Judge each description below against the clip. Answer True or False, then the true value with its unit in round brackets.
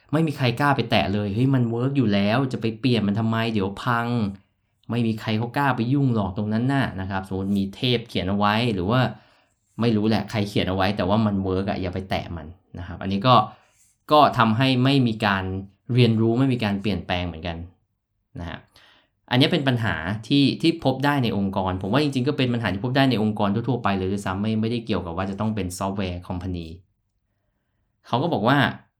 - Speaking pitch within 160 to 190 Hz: False (105 Hz)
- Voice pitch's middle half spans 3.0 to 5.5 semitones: True (3.7 semitones)